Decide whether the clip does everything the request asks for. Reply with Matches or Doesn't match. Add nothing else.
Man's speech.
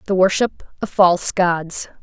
Doesn't match